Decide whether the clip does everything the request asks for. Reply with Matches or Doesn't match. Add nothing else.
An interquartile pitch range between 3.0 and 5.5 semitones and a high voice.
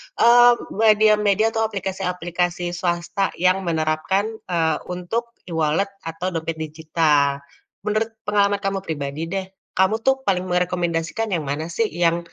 Doesn't match